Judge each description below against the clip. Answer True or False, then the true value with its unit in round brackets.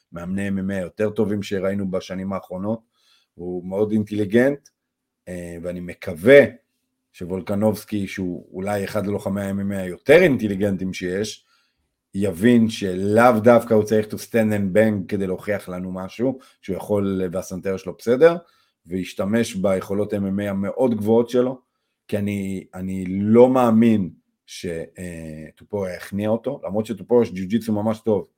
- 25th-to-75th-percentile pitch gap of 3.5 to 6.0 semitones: False (3.1 semitones)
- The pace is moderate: True (125 wpm)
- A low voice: True (100 Hz)